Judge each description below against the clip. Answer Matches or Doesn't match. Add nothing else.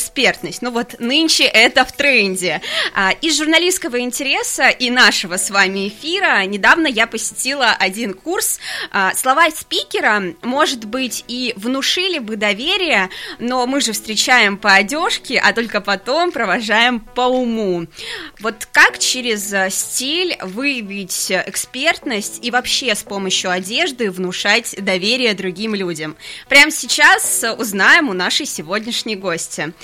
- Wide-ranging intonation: Matches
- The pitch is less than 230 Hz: Doesn't match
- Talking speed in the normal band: Matches